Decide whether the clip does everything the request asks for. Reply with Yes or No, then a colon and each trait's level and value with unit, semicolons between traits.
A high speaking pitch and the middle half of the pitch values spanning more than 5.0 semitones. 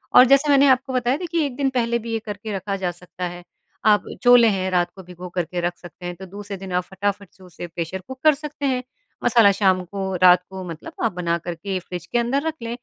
Yes: high, 195 Hz; wide, 5.4 semitones